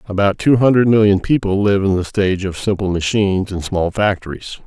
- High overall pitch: No, low, 100 Hz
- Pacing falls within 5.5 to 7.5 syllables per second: Yes, 5.6 syllables/s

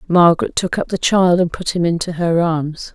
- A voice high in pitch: No, medium, 170 Hz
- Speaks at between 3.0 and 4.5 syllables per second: No, 5.1 syllables/s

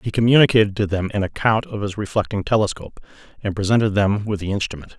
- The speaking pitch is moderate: No, low, 105 Hz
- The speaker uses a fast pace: No, average, 195 wpm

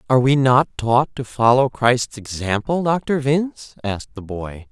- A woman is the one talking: No, male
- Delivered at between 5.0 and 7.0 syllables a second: No, 4.4 syllables/s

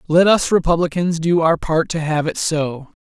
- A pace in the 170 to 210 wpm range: Yes, average, 200 wpm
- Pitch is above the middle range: No, medium, 165 Hz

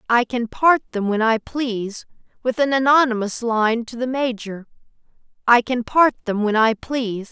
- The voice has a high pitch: Yes, high, 235 Hz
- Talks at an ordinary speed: Yes, average, 170 wpm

